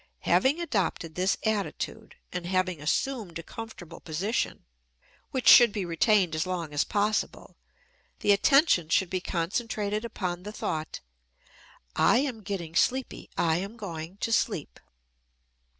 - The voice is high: Yes, high, 195 Hz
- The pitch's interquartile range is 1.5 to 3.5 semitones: No, average, 4.7 semitones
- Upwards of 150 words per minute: No, slow, 135 wpm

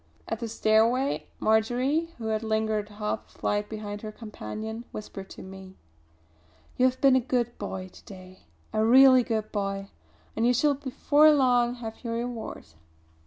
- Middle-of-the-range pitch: No, high, 220 Hz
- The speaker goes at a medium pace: Yes, average, 165 wpm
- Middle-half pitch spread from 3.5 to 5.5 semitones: No, average, 2.9 semitones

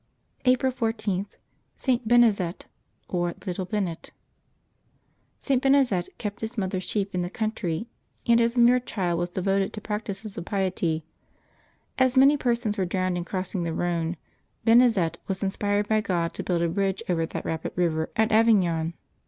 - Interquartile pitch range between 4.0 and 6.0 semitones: Yes, average, 4.4 semitones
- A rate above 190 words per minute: No, average, 160 wpm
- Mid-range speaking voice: No, high, 195 Hz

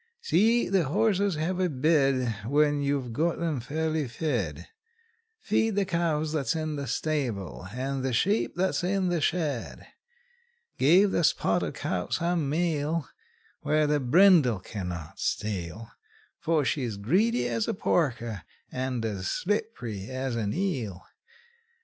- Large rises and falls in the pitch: Yes, wide, 6.3 semitones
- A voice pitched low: No, medium, 145 Hz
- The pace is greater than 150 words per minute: No, slow, 135 wpm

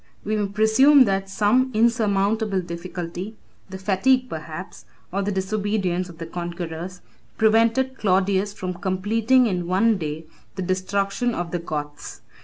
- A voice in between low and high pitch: No, high, 195 Hz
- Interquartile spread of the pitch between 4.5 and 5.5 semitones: No, average, 3.4 semitones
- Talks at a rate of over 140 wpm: No, slow, 135 wpm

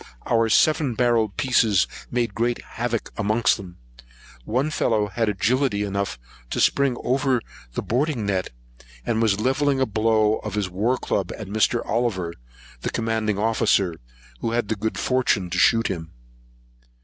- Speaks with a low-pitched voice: Yes, low, 110 Hz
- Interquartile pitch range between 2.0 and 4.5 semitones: Yes, average, 3.1 semitones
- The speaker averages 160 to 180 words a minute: No, average, 150 wpm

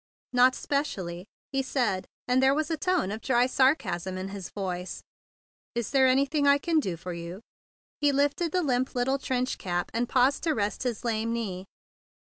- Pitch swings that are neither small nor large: No, wide, 6.3 semitones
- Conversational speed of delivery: Yes, average, 180 wpm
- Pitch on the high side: Yes, very high, 250 Hz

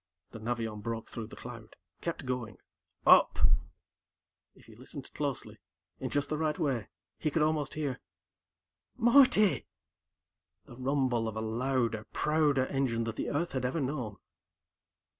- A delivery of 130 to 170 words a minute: Yes, average, 140 wpm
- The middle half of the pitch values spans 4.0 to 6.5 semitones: Yes, average, 4.8 semitones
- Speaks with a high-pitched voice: No, low, 130 Hz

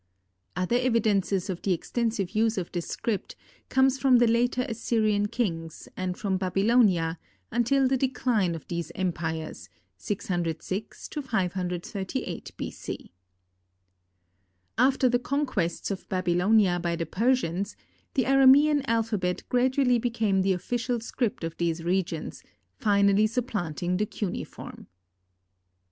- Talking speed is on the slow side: Yes, slow, 120 wpm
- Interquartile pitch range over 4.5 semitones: Yes, average, 5.2 semitones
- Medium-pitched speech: No, high, 205 Hz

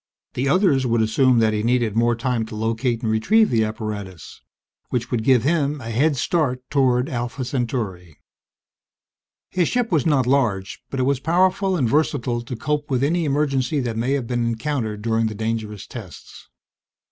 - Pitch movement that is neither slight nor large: Yes, average, 3.9 semitones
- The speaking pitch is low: Yes, low, 125 Hz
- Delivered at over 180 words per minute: No, average, 175 wpm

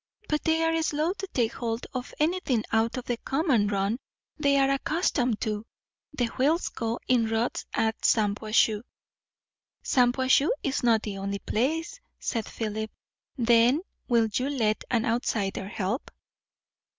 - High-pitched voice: Yes, high, 240 Hz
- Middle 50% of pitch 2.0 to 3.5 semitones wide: No, average, 3.9 semitones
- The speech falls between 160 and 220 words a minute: No, average, 140 wpm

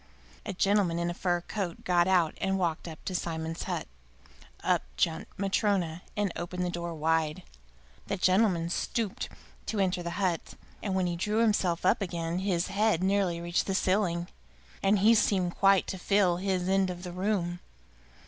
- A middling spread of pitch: No, narrow, 2.3 semitones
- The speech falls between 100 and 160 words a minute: No, average, 175 wpm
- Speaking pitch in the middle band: Yes, medium, 180 Hz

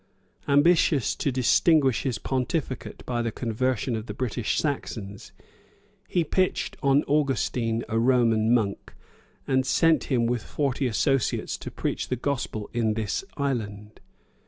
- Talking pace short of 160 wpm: Yes, slow, 135 wpm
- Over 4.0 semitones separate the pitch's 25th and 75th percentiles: No, average, 3.7 semitones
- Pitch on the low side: Yes, low, 125 Hz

